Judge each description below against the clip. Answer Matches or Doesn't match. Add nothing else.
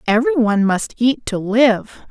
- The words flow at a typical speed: Matches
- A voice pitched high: Matches